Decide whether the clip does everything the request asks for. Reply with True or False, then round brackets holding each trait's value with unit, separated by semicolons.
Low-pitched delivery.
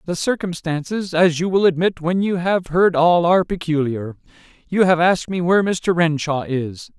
False (170 Hz)